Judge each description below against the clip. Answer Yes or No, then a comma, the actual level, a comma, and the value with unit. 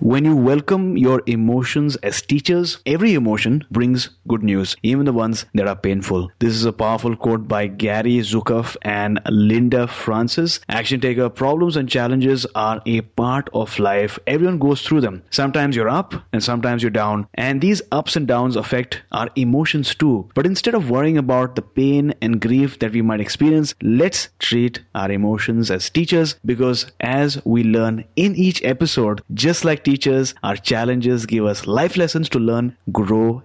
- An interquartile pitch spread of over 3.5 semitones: Yes, average, 4.1 semitones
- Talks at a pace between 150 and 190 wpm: Yes, average, 175 wpm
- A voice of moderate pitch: No, low, 120 Hz